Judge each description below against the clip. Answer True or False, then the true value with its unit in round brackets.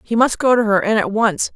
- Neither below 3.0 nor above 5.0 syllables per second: False (5.5 syllables/s)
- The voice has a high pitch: True (215 Hz)